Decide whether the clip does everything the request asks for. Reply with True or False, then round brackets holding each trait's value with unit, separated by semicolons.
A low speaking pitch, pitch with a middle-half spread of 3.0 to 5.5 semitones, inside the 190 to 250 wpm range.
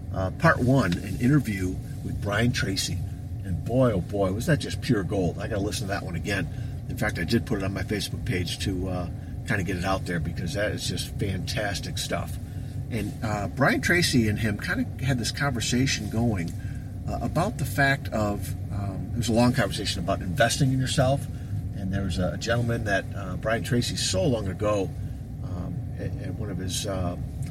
True (105 Hz; 4.2 semitones; 205 wpm)